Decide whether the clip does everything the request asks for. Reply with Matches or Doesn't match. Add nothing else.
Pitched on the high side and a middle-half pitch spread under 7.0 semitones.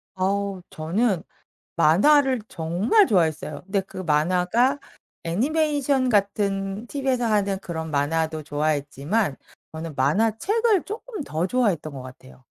Doesn't match